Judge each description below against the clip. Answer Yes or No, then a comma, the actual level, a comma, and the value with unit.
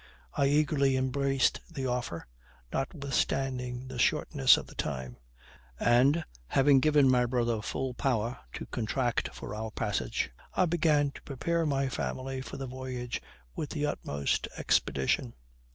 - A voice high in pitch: No, low, 130 Hz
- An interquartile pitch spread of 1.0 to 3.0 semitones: Yes, narrow, 2.6 semitones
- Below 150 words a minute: Yes, slow, 135 wpm